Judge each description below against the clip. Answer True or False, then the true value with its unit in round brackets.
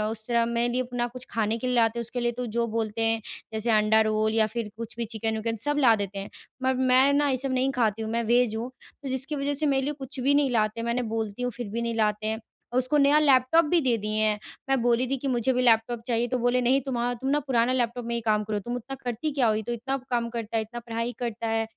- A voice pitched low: False (235 Hz)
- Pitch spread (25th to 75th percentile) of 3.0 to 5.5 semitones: False (2.4 semitones)